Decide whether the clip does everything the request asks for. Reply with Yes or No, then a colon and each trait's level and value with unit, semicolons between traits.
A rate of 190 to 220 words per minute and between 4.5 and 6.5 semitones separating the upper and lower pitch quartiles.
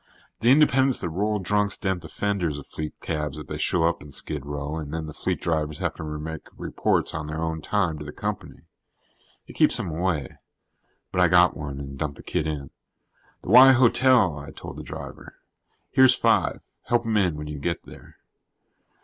Yes: average, 200 wpm; average, 5.1 semitones